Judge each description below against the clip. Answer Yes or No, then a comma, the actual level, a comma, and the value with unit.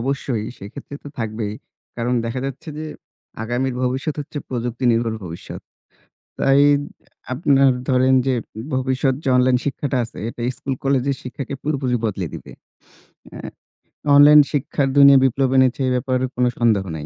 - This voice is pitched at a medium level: No, low, 130 Hz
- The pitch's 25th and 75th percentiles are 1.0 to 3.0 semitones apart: Yes, narrow, 2.4 semitones